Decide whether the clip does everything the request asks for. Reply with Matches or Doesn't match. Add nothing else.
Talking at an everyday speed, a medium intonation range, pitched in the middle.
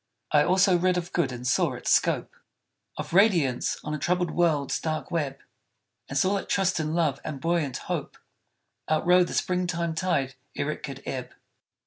Matches